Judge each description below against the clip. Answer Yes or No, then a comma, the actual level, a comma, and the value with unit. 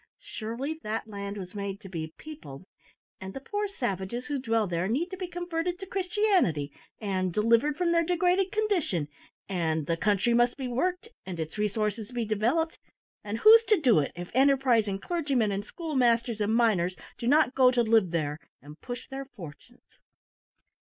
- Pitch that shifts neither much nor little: No, wide, 8.2 semitones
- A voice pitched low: No, high, 235 Hz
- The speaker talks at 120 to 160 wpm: No, average, 170 wpm